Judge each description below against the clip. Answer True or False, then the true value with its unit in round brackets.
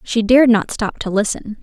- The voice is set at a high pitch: True (220 Hz)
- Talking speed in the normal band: False (220 wpm)